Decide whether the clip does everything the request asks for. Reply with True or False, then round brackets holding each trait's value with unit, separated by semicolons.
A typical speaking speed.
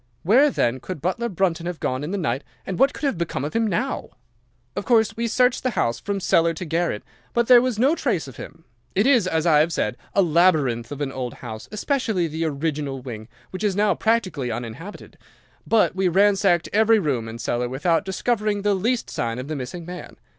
False (210 wpm)